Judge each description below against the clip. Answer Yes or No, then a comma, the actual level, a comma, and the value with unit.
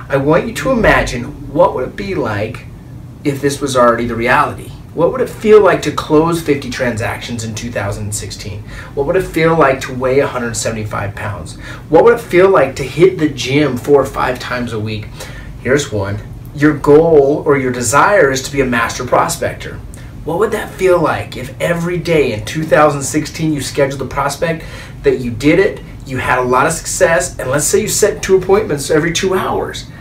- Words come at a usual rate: Yes, average, 195 wpm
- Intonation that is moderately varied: Yes, average, 4.0 semitones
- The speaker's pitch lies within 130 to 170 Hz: Yes, low, 135 Hz